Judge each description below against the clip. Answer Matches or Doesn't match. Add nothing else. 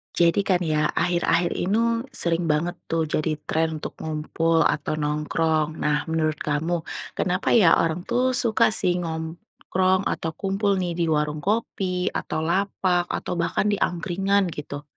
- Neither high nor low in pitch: Matches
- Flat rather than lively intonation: Doesn't match